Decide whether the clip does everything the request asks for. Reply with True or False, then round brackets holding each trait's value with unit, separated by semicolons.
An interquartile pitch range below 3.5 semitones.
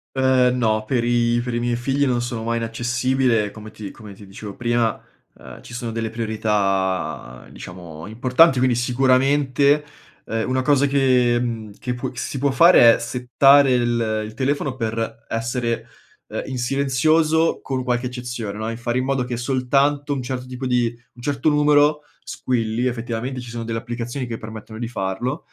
True (2.4 semitones)